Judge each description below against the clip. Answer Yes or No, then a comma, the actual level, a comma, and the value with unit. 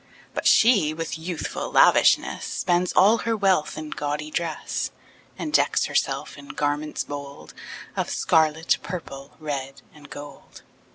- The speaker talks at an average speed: No, slow, 130 wpm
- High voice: No, medium, 155 Hz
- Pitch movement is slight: No, average, 3.7 semitones